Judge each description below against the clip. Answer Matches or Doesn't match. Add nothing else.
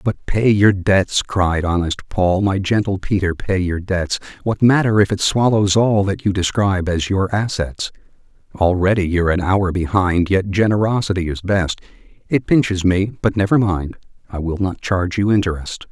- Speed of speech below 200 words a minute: Matches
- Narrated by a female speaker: Doesn't match